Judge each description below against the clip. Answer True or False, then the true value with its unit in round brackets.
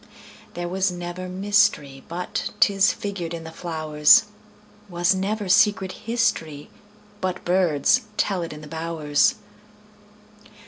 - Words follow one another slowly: True (100 wpm)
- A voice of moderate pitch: True (180 Hz)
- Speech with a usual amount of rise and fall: True (3.9 semitones)